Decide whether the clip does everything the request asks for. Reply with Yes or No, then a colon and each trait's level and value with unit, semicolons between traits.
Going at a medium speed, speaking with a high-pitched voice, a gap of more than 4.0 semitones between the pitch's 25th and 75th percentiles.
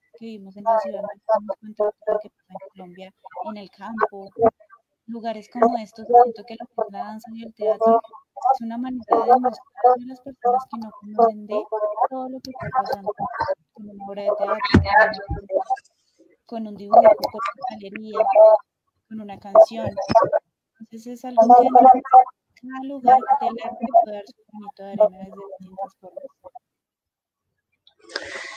No: average, 150 wpm; high, 225 Hz; average, 3.7 semitones